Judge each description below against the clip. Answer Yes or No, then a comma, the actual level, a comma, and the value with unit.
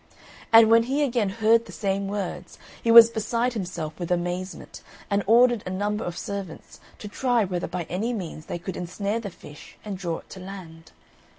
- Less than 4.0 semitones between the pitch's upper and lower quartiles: No, average, 4.3 semitones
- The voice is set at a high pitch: Yes, high, 200 Hz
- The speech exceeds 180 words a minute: Yes, average, 190 wpm